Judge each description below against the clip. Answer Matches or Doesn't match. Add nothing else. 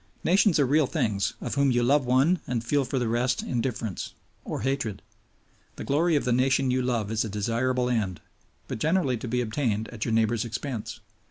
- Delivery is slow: Doesn't match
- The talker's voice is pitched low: Matches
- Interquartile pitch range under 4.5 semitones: Matches